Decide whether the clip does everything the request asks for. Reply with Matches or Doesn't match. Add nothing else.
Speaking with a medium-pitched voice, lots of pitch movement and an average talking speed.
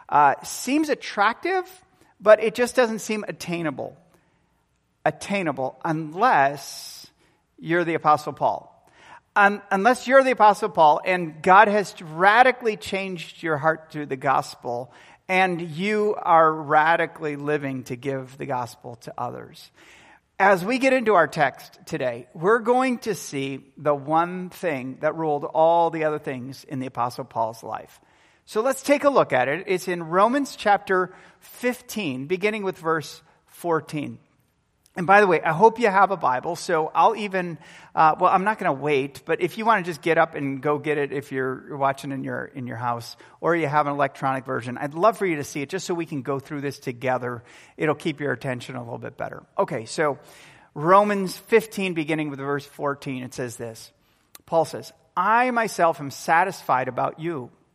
Matches